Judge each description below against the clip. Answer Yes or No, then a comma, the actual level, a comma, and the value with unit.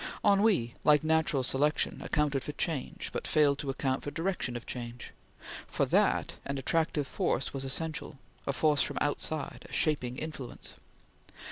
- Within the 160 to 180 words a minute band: No, average, 150 wpm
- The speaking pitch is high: No, medium, 145 Hz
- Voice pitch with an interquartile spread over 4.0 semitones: No, average, 2.9 semitones